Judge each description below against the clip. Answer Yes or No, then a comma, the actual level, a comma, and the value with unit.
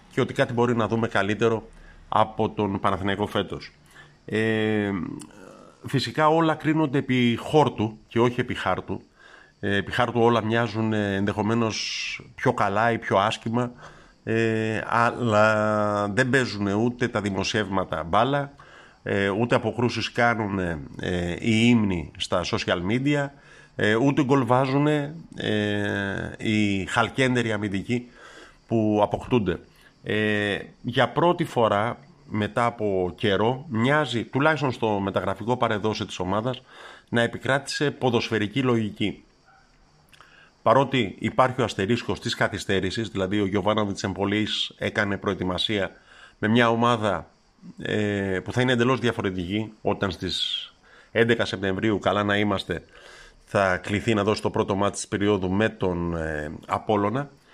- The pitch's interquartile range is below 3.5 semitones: Yes, average, 3.1 semitones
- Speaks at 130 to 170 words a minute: No, average, 120 wpm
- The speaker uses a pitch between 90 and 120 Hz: Yes, low, 110 Hz